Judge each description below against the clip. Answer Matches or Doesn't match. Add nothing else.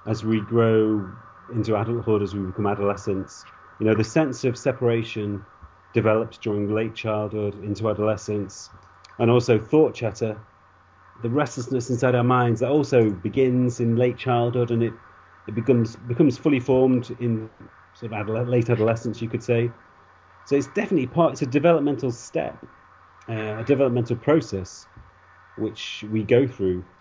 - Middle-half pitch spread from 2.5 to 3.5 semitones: Matches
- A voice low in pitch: Matches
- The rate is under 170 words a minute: Matches